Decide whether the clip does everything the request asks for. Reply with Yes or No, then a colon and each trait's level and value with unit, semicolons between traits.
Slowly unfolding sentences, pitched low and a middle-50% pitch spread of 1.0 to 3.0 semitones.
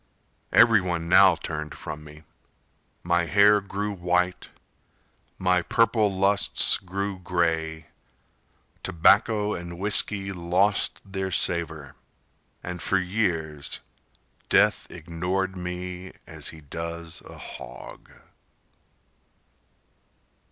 Yes: slow, 90 wpm; very low, 90 Hz; average, 2.7 semitones